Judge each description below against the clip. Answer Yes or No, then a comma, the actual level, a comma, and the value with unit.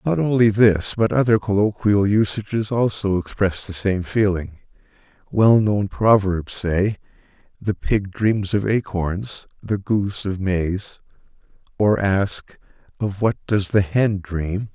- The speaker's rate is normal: No, slow, 130 wpm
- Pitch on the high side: No, low, 100 Hz